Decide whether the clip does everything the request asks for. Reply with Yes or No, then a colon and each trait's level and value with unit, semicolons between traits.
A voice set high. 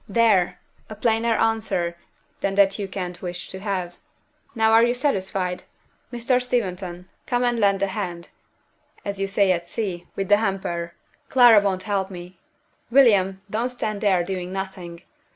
Yes: high, 195 Hz